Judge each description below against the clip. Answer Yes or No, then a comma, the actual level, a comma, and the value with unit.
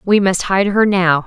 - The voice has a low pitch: No, high, 190 Hz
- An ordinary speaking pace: No, fast, 240 wpm